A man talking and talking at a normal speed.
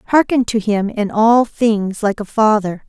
No: female; average, 190 wpm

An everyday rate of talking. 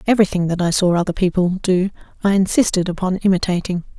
Yes: average, 165 wpm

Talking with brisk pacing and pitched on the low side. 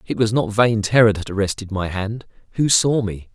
Yes: fast, 215 wpm; low, 105 Hz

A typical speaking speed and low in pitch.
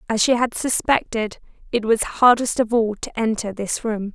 No: average, 190 wpm; high, 225 Hz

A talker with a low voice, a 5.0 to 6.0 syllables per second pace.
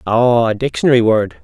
Yes: low, 115 Hz; 5.4 syllables/s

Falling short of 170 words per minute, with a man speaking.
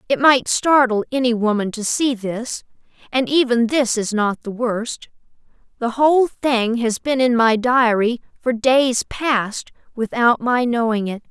No: average, 160 wpm; female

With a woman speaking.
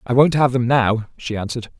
No: male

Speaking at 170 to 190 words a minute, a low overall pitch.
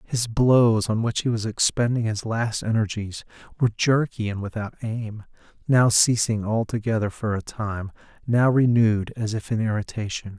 No: average, 155 wpm; low, 110 Hz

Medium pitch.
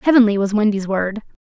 No: high, 210 Hz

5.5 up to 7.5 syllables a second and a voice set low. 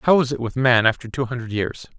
Yes: 5.9 syllables/s; low, 125 Hz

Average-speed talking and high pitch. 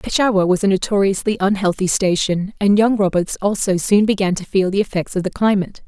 Yes: average, 195 wpm; high, 195 Hz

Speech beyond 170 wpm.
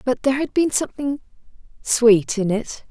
No: average, 165 wpm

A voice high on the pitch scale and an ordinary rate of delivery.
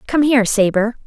Yes: high, 235 Hz; average, 170 wpm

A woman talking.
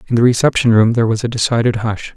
No: male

